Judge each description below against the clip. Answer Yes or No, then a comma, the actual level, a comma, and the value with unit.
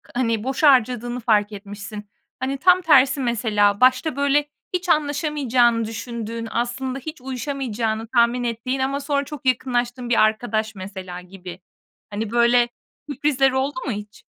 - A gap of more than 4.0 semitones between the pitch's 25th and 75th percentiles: No, average, 3.6 semitones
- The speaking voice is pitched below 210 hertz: No, high, 245 Hz